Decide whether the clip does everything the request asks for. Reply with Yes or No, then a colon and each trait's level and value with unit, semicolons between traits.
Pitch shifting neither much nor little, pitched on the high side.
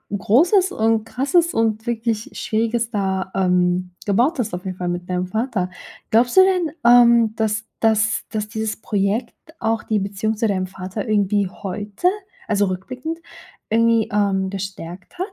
Yes: average, 3.2 semitones; high, 215 Hz